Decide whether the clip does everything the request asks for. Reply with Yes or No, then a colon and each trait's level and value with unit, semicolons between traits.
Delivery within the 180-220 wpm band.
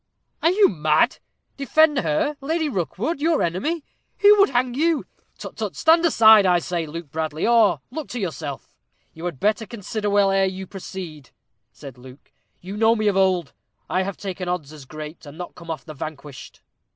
Yes: average, 185 wpm